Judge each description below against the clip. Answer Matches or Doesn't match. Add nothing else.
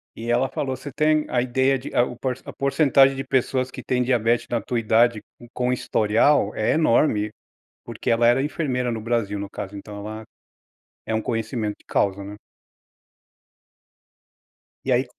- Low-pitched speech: Matches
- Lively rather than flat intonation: Doesn't match